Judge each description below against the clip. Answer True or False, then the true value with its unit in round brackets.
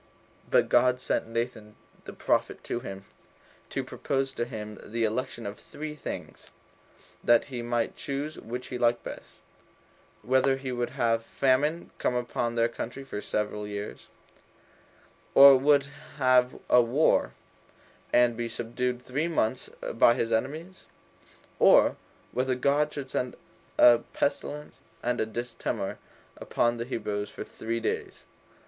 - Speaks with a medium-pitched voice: False (120 Hz)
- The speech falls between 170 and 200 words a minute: False (140 wpm)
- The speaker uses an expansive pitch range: False (2.5 semitones)